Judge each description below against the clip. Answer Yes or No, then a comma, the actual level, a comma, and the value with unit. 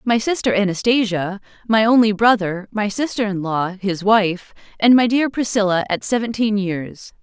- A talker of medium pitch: No, high, 210 Hz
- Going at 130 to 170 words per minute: Yes, average, 160 wpm